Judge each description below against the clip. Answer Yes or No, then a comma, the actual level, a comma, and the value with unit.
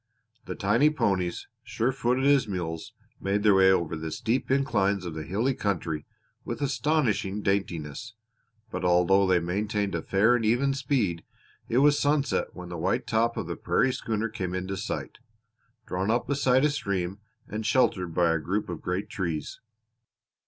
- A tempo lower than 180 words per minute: Yes, average, 165 wpm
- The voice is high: No, low, 100 Hz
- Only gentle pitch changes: No, wide, 5.4 semitones